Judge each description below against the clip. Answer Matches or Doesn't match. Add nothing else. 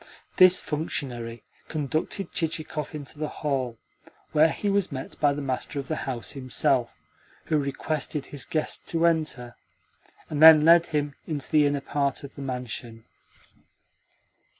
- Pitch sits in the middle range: Matches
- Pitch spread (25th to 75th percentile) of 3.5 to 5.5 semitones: Doesn't match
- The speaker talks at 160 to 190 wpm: Doesn't match